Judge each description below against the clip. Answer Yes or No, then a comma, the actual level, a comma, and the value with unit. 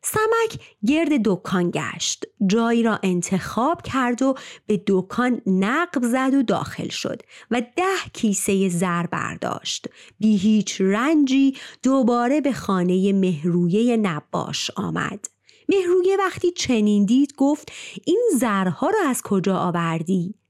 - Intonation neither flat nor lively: No, wide, 6.3 semitones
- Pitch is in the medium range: No, high, 230 Hz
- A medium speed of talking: Yes, average, 120 wpm